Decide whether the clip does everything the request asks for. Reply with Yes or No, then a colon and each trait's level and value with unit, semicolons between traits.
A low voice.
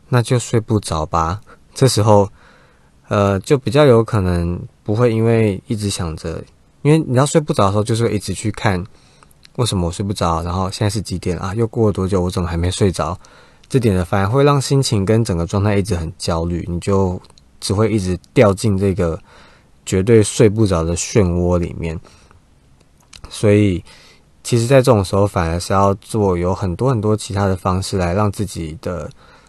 Yes: low, 100 Hz